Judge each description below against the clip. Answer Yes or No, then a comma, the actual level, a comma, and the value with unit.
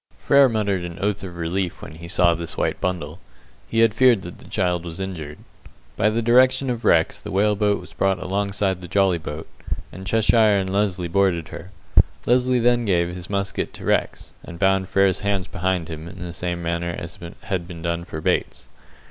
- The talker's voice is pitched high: No, very low, 95 Hz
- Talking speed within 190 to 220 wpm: Yes, average, 200 wpm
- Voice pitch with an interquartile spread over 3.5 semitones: No, average, 3.0 semitones